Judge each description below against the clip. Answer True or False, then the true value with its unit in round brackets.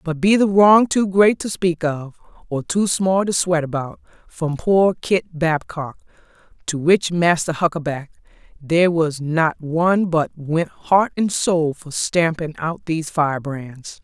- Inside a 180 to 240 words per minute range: False (160 wpm)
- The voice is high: False (170 Hz)